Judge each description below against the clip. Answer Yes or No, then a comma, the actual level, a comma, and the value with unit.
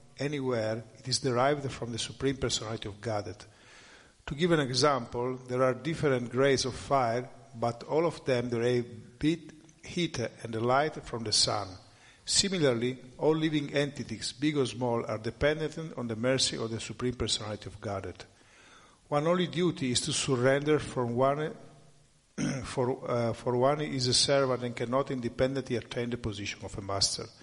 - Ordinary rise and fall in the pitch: Yes, average, 3.5 semitones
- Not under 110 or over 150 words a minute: No, average, 160 wpm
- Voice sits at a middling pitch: No, low, 125 Hz